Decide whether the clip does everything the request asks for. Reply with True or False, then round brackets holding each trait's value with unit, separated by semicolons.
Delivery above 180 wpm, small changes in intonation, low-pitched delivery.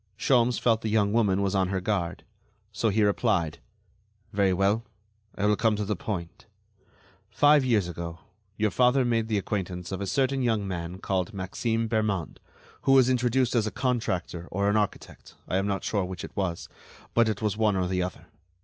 False (190 wpm; 3.4 semitones; 105 Hz)